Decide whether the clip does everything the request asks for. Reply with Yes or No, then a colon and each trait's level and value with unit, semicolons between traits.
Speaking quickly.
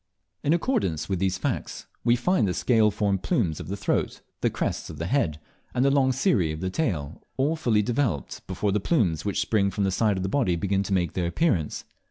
Yes: fast, 225 wpm